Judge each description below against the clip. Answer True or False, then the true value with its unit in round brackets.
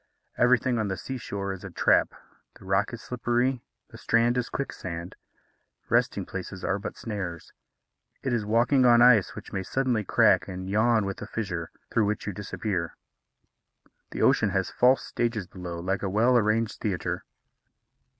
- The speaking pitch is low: True (105 Hz)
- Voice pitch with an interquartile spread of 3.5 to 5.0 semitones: True (3.8 semitones)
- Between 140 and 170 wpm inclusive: True (165 wpm)